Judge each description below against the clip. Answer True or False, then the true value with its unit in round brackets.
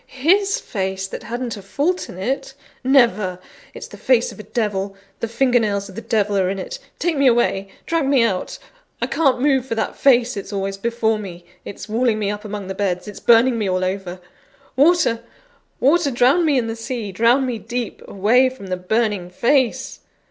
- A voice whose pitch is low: False (230 Hz)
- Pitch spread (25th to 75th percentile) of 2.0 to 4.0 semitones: False (4.6 semitones)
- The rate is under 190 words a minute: False (200 wpm)